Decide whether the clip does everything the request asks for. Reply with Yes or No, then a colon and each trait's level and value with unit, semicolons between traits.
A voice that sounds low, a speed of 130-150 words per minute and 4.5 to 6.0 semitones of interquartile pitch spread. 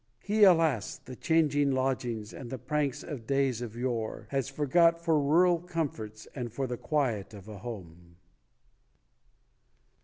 Yes: low, 130 Hz; average, 145 wpm; average, 5.0 semitones